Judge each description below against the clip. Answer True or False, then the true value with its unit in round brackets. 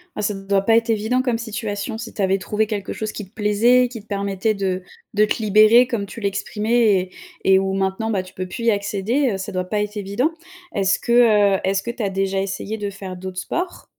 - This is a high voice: True (205 Hz)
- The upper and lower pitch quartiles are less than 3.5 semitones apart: True (2.5 semitones)